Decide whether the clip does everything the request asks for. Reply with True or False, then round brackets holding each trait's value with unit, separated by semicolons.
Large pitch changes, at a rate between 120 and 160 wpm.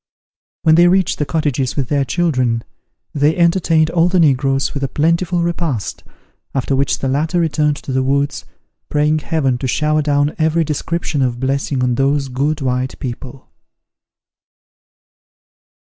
False (3.2 semitones; 145 wpm)